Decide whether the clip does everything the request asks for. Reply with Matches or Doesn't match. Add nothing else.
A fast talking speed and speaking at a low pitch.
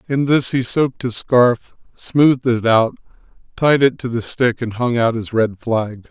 Doesn't match